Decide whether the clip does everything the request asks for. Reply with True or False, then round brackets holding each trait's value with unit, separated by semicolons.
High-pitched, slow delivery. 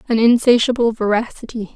True (230 Hz; 100 wpm)